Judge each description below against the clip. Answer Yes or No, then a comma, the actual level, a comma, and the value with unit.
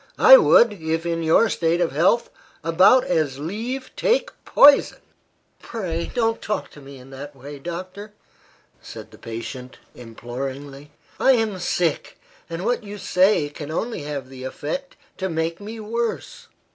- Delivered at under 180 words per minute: Yes, average, 150 wpm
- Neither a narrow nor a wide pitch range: No, wide, 7.3 semitones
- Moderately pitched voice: Yes, medium, 170 Hz